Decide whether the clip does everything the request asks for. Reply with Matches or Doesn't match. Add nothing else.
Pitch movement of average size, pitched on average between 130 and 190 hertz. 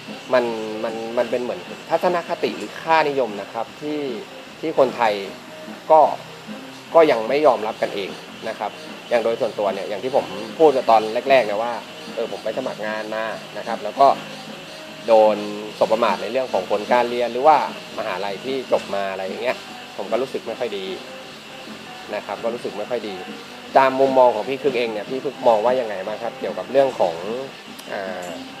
Doesn't match